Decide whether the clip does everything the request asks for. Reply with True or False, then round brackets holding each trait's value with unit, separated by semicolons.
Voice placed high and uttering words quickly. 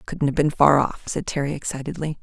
False (145 Hz; 245 wpm)